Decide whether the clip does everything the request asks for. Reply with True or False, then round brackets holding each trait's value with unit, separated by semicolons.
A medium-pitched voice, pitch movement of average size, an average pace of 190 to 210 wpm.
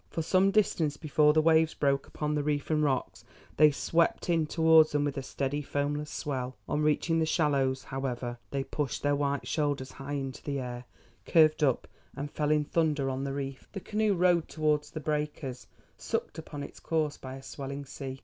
False (145 Hz; 2.3 semitones; 195 wpm)